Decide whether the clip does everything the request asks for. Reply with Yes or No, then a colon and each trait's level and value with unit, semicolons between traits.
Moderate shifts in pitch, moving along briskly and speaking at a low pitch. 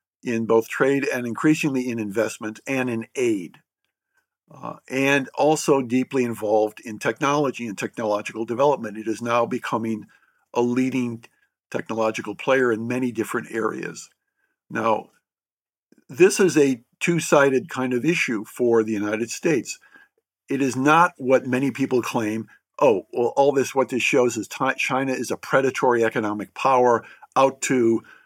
No: average, 3.7 semitones; average, 145 wpm; low, 130 Hz